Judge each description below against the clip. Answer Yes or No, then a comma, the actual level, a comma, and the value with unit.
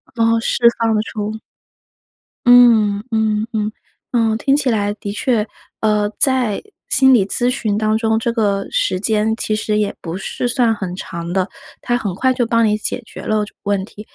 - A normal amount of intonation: No, narrow, 2.0 semitones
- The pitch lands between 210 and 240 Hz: Yes, high, 220 Hz